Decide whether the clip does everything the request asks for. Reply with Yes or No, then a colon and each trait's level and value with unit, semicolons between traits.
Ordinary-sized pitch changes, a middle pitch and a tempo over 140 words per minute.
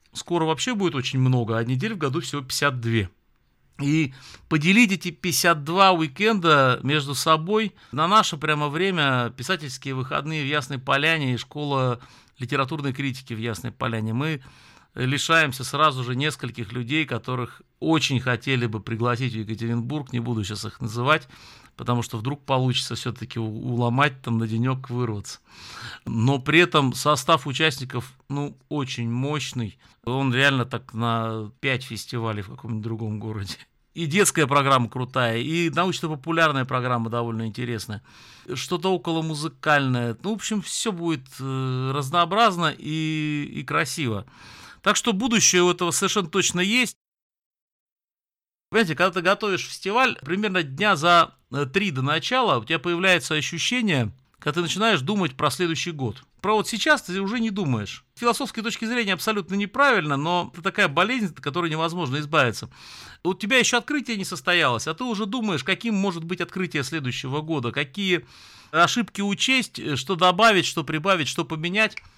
No: wide, 6.3 semitones; medium, 150 Hz; average, 150 wpm